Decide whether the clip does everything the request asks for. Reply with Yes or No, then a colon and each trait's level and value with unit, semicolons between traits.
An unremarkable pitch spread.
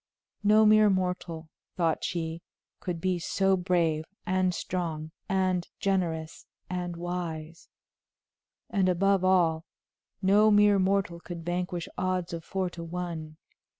No: narrow, 2.1 semitones